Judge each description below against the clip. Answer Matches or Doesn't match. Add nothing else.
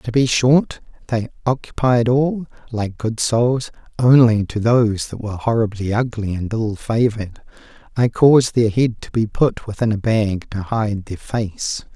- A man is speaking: Matches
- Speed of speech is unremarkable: Matches